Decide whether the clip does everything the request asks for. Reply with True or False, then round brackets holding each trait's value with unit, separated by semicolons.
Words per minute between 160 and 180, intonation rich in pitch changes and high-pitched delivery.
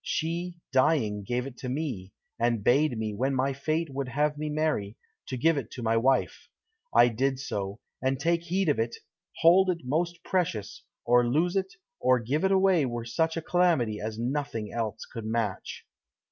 False (175 wpm; 5.8 semitones; 135 Hz)